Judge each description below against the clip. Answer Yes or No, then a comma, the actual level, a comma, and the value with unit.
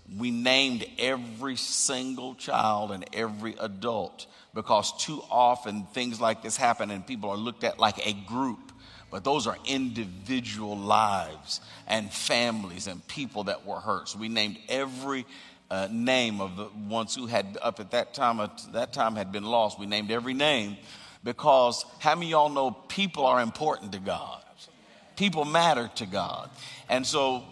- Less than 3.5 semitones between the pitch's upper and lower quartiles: No, average, 3.8 semitones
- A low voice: Yes, low, 120 Hz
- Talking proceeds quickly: No, average, 170 wpm